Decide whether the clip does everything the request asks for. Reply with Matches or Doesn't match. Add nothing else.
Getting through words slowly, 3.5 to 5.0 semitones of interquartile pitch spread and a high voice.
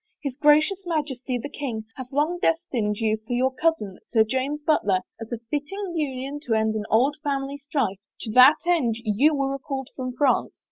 Doesn't match